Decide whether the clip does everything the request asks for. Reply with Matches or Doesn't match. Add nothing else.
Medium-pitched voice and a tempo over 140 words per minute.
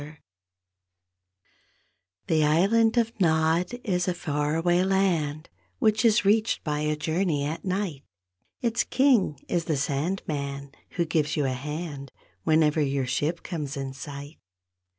Doesn't match